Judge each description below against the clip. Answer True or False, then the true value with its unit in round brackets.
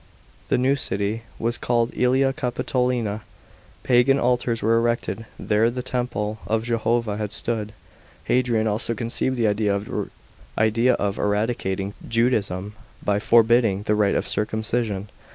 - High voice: False (115 Hz)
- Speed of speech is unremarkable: False (125 wpm)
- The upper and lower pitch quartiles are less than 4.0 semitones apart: True (2.6 semitones)